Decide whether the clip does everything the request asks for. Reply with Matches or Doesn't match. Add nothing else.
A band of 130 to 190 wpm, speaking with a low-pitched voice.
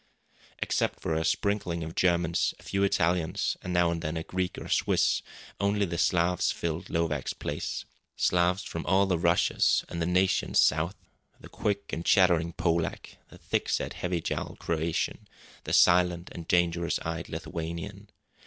Matches